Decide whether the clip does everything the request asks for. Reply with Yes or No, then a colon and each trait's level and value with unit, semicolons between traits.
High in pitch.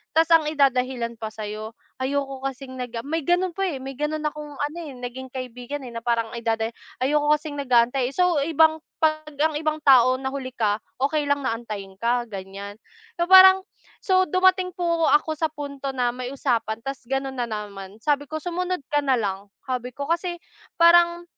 Yes: very high, 275 Hz